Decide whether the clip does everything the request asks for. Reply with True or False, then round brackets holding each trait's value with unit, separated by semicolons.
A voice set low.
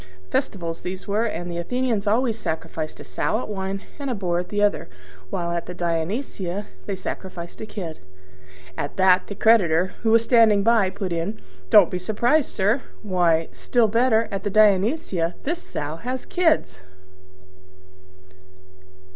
False (195 Hz)